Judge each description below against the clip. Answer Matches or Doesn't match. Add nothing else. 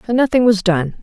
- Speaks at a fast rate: Matches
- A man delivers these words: Doesn't match